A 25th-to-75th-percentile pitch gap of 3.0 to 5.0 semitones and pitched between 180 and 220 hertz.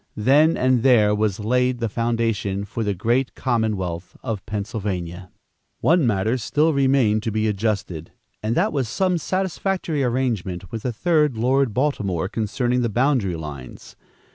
No: average, 4.5 semitones; low, 115 Hz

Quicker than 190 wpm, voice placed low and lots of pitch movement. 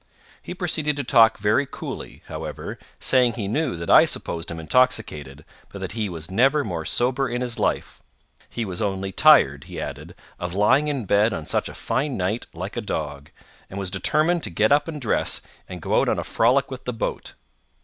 Yes: average, 200 wpm; low, 110 Hz; wide, 6.6 semitones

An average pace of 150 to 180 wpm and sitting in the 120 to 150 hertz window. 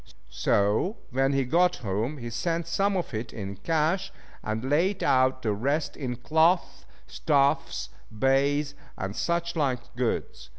No: average, 140 wpm; low, 135 Hz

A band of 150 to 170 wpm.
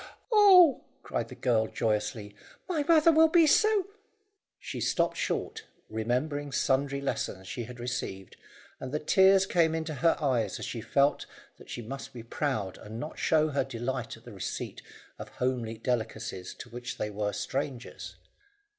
Yes: average, 165 wpm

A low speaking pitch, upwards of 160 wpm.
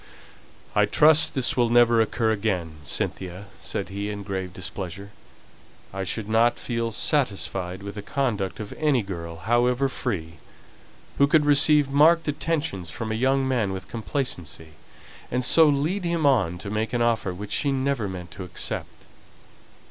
No: low, 110 Hz; average, 155 wpm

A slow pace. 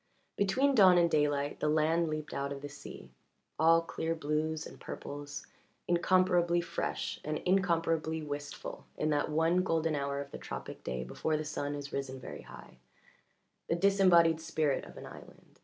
No: average, 170 wpm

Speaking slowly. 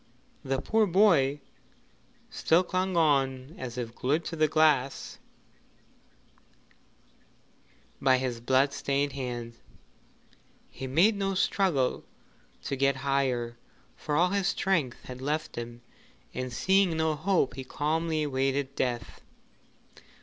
Yes: slow, 115 wpm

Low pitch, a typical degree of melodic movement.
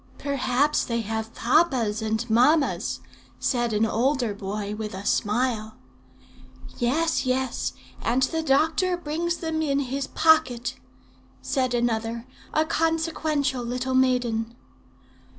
No: very high, 255 Hz; average, 4.9 semitones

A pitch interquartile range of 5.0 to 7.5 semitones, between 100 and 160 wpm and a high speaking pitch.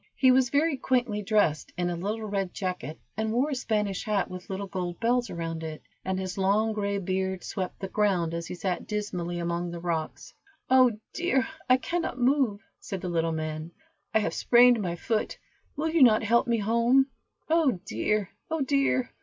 No: wide, 5.4 semitones; average, 185 wpm; high, 205 Hz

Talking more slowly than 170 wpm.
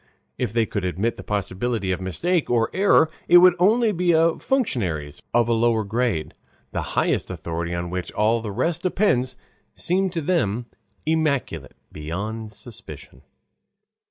Yes: average, 150 wpm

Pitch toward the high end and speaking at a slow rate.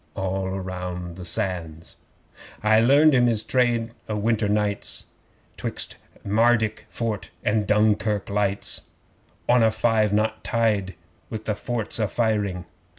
No: low, 105 Hz; slow, 130 wpm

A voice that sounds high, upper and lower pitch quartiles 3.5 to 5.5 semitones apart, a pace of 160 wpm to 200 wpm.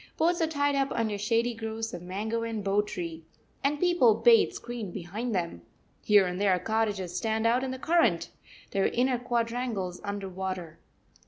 Yes: high, 220 Hz; average, 4.0 semitones; average, 170 wpm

